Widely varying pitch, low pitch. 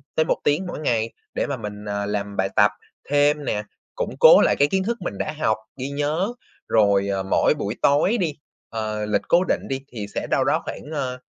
Yes: wide, 6.7 semitones; low, 130 Hz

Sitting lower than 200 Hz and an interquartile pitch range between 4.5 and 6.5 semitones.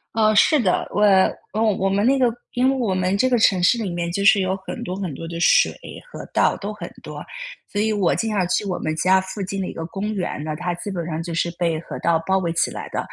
No: high, 190 Hz; average, 3.5 semitones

